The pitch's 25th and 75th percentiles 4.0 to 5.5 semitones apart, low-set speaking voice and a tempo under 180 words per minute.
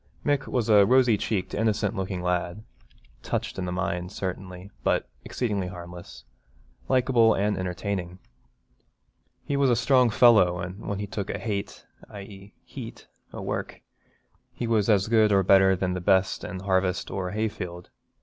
No: average, 3.2 semitones; low, 100 Hz; average, 155 wpm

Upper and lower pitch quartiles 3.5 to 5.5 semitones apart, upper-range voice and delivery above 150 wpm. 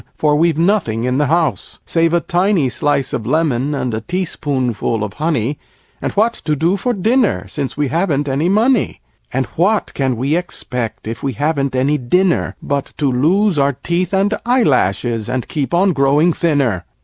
No: average, 5.2 semitones; medium, 150 Hz; average, 175 wpm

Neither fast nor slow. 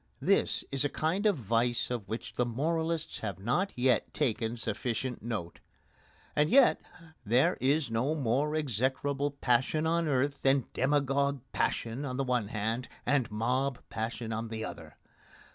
Yes: average, 150 wpm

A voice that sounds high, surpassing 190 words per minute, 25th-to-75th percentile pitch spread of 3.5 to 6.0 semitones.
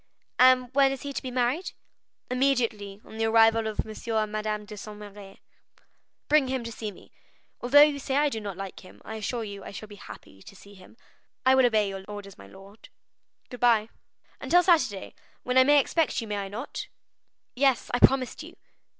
Yes: high, 225 Hz; average, 200 wpm; average, 4.0 semitones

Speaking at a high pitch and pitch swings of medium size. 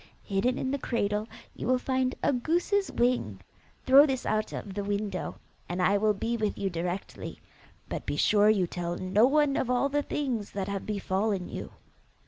Yes: high, 215 Hz; average, 4.8 semitones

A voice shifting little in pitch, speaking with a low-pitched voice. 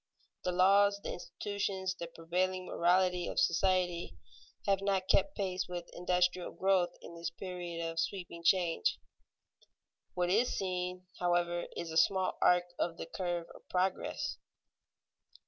No: narrow, 1.5 semitones; medium, 180 Hz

